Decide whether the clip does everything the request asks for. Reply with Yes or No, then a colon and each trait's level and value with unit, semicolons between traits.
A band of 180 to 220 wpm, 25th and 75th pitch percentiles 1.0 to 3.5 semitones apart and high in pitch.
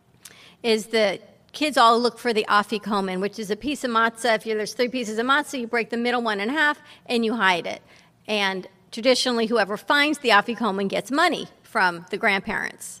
Yes: average, 195 wpm; average, 3.0 semitones; high, 225 Hz